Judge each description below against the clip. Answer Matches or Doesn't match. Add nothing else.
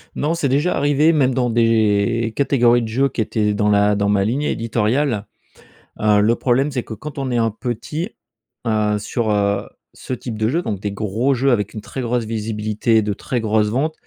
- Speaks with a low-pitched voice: Matches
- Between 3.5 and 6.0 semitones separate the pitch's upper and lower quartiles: Matches